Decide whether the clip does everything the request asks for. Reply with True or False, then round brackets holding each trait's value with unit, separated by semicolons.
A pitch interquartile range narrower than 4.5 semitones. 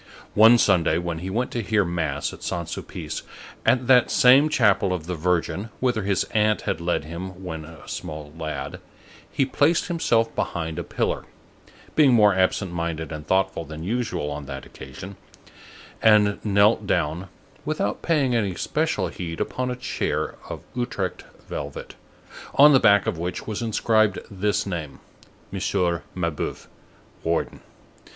False (5.2 semitones)